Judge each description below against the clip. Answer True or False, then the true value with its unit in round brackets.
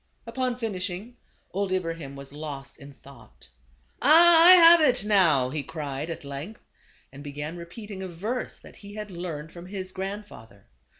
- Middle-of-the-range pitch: True (180 Hz)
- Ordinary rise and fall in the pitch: False (6.6 semitones)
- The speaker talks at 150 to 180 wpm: True (170 wpm)